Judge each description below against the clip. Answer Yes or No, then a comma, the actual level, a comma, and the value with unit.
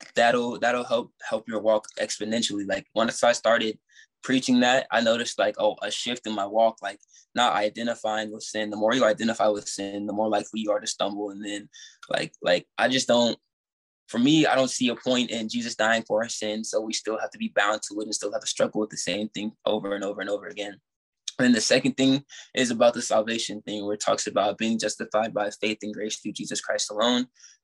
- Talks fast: Yes, fast, 235 wpm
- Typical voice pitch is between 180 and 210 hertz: No, low, 110 Hz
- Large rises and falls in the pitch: No, narrow, 2.4 semitones